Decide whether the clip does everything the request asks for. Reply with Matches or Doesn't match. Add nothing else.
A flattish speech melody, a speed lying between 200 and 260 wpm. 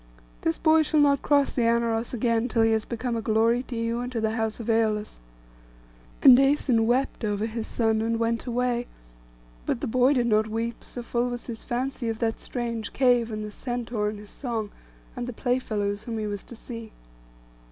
Matches